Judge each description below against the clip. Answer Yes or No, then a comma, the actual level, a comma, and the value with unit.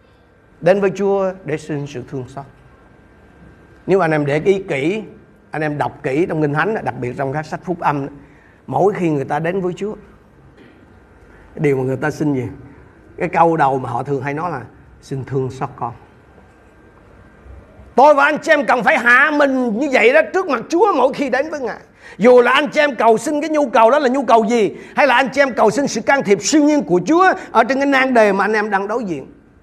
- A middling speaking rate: Yes, average, 230 wpm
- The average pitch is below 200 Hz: Yes, medium, 185 Hz